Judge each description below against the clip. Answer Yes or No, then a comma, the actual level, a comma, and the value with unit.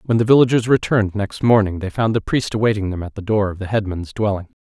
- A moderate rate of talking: No, fast, 245 wpm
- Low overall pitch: Yes, low, 105 Hz